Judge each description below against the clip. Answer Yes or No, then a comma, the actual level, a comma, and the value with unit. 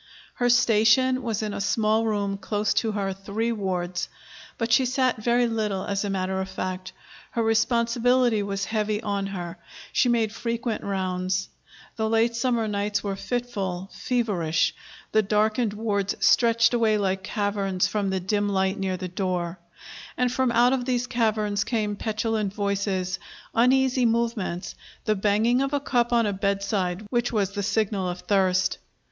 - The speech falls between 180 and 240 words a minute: No, average, 160 wpm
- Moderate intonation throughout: Yes, average, 3.2 semitones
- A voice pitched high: Yes, high, 210 Hz